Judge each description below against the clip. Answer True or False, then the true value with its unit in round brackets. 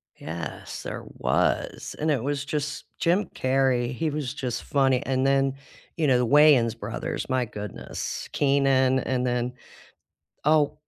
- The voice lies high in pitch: False (135 Hz)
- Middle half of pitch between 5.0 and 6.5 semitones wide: False (2.7 semitones)